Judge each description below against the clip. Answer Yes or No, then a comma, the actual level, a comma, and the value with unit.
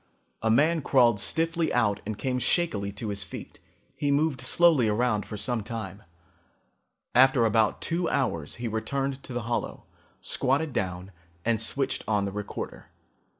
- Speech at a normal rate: Yes, average, 150 wpm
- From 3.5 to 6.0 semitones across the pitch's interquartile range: Yes, average, 4.8 semitones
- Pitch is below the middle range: Yes, low, 120 Hz